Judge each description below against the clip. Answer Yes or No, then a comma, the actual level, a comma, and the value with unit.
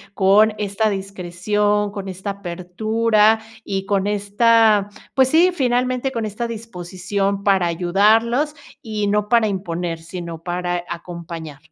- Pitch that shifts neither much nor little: Yes, average, 3.5 semitones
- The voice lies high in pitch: Yes, high, 200 Hz